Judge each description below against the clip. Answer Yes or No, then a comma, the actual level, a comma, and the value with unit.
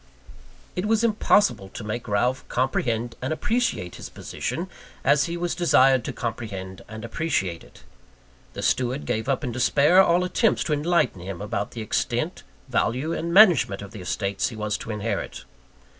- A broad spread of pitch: Yes, wide, 8.0 semitones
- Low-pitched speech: Yes, low, 125 Hz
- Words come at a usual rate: Yes, average, 165 wpm